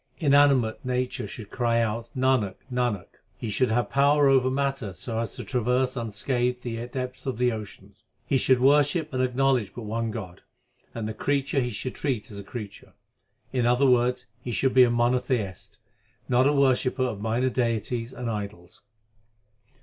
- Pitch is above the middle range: No, low, 125 Hz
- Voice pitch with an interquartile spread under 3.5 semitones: Yes, narrow, 2.5 semitones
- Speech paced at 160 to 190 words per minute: Yes, average, 170 wpm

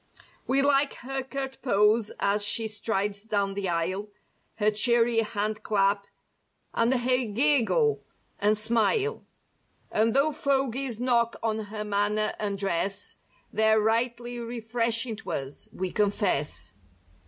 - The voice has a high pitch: Yes, high, 220 Hz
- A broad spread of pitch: No, average, 3.0 semitones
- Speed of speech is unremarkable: No, slow, 125 wpm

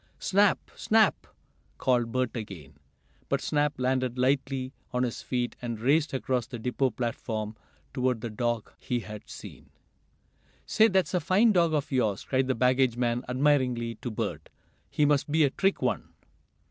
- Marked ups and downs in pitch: No, average, 3.6 semitones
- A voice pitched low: Yes, low, 130 Hz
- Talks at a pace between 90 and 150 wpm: No, average, 160 wpm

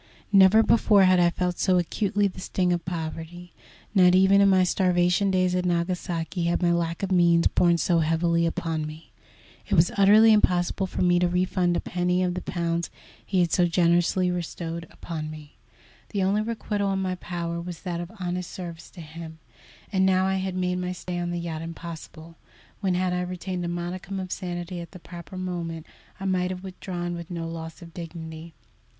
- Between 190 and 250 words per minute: Yes, average, 195 wpm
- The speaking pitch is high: No, medium, 175 Hz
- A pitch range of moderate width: No, narrow, 1.6 semitones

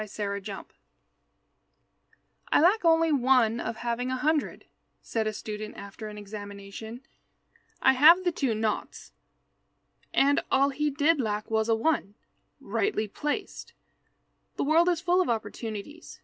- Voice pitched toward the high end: Yes, high, 240 Hz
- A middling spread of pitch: No, wide, 6.2 semitones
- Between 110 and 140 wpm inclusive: Yes, slow, 135 wpm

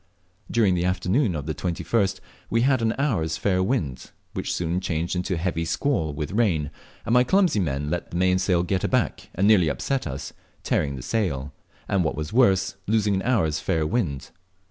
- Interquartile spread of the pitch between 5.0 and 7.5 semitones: Yes, wide, 5.5 semitones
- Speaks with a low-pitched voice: Yes, very low, 90 Hz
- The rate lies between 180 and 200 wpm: Yes, average, 190 wpm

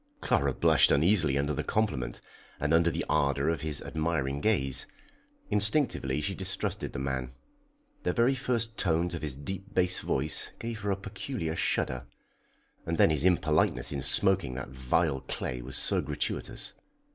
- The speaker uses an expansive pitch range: Yes, wide, 6.2 semitones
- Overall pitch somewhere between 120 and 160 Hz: No, very low, 80 Hz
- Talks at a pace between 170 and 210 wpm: No, average, 160 wpm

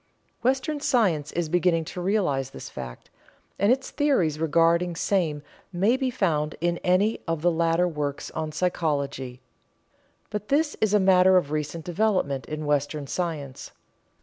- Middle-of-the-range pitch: Yes, medium, 170 Hz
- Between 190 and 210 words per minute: No, average, 150 wpm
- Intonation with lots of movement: No, average, 4.7 semitones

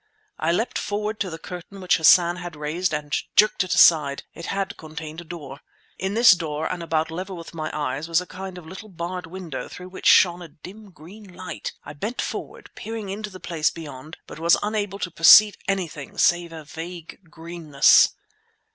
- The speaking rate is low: No, average, 190 wpm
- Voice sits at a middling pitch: Yes, medium, 175 Hz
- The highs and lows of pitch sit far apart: No, average, 3.2 semitones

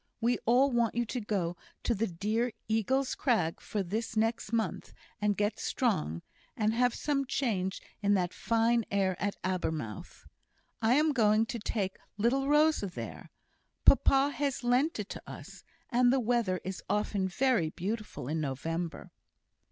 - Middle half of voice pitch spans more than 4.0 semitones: Yes, average, 4.4 semitones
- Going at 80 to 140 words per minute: No, average, 155 wpm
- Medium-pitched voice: No, high, 220 Hz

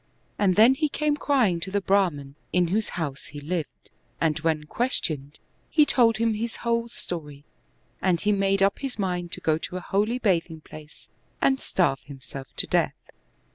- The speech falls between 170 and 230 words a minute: Yes, average, 175 wpm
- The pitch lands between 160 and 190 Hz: Yes, medium, 185 Hz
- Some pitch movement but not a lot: No, wide, 6.5 semitones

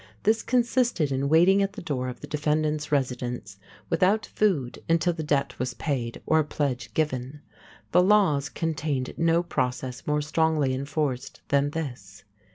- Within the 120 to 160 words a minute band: Yes, average, 155 wpm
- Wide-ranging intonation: No, average, 4.1 semitones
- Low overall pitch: No, medium, 150 Hz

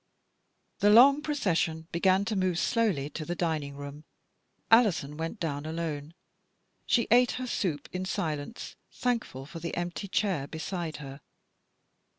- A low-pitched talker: No, medium, 170 Hz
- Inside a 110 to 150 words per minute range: Yes, average, 140 wpm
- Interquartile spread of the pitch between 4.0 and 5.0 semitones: No, wide, 5.5 semitones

